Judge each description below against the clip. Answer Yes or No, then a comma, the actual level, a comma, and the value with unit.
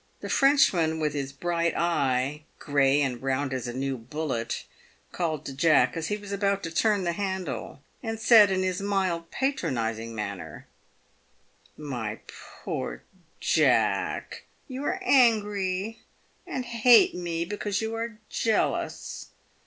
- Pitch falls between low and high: Yes, medium, 170 Hz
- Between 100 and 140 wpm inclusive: Yes, slow, 135 wpm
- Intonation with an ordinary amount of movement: No, wide, 7.2 semitones